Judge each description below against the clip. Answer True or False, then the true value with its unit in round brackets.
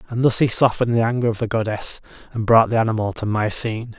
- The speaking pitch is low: True (115 Hz)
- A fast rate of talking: True (225 wpm)